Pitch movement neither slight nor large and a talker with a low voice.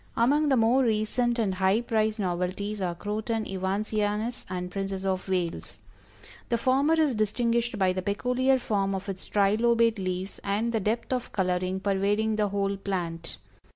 No: average, 3.4 semitones; high, 210 Hz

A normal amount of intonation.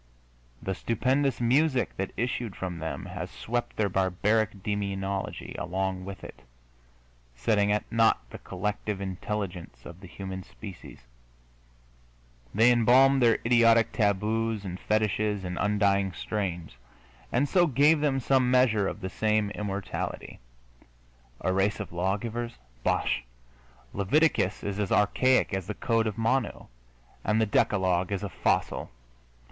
Yes: average, 3.4 semitones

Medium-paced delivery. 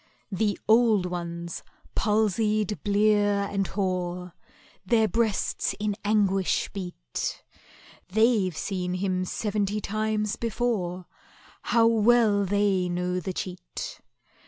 No: slow, 100 wpm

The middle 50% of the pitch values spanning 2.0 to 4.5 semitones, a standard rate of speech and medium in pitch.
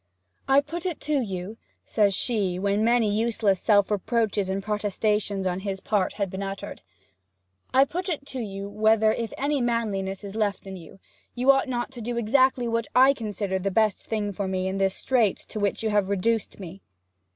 No: average, 3.3 semitones; average, 195 wpm; high, 210 Hz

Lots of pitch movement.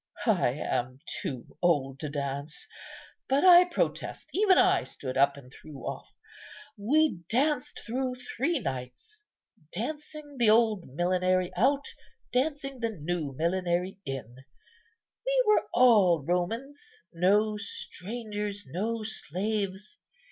Yes: wide, 8.2 semitones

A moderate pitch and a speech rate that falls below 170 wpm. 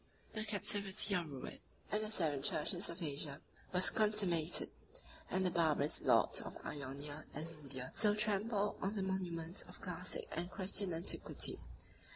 Yes: medium, 180 Hz; average, 150 wpm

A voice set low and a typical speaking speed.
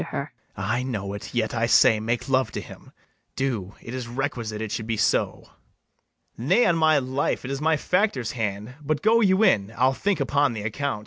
No: low, 125 Hz; fast, 215 wpm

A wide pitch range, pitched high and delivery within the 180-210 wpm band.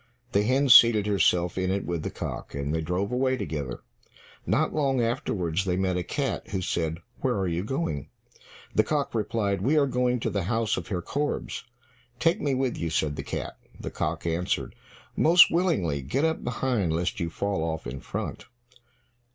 No: wide, 7.2 semitones; low, 100 Hz; average, 185 wpm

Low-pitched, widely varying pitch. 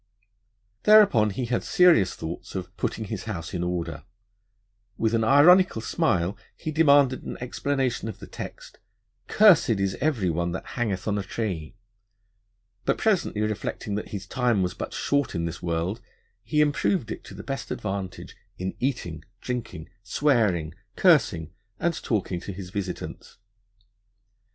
Yes: low, 105 Hz; wide, 6.9 semitones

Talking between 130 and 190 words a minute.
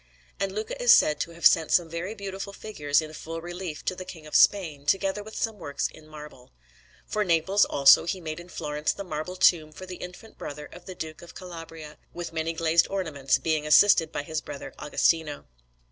No: fast, 205 wpm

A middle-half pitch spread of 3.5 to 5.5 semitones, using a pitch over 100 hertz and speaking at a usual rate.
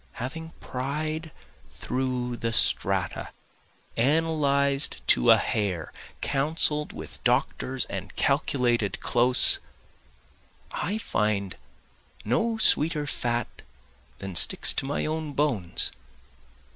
No: average, 4.4 semitones; low, 135 Hz; slow, 95 wpm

